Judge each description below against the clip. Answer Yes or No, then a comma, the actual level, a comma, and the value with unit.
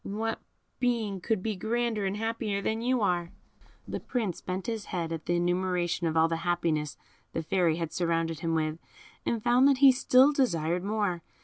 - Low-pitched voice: No, high, 190 Hz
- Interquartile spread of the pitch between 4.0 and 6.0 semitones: Yes, average, 5.1 semitones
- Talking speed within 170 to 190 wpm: Yes, average, 185 wpm